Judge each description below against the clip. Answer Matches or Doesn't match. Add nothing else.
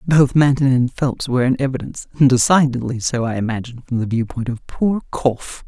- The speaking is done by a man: Doesn't match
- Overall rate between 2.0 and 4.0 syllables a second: Doesn't match